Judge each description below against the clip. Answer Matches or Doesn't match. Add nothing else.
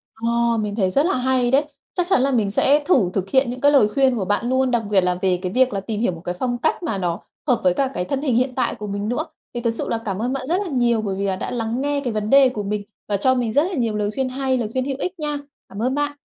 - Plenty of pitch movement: Doesn't match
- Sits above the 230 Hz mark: Matches